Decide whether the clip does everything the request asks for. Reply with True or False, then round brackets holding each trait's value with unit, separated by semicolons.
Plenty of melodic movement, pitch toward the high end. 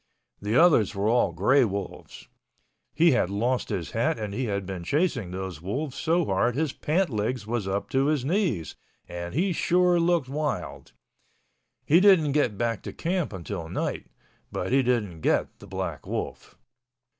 False (7.7 semitones; 125 Hz)